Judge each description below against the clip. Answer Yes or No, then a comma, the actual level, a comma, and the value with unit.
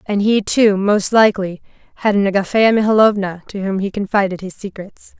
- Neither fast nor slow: Yes, average, 175 wpm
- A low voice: No, high, 200 Hz